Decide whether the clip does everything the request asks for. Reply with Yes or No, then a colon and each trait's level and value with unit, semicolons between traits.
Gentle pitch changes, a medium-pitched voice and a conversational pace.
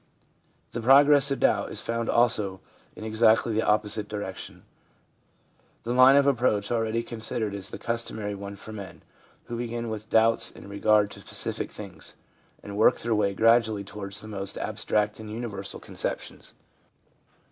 No: narrow, 2.3 semitones; low, 110 Hz; average, 160 wpm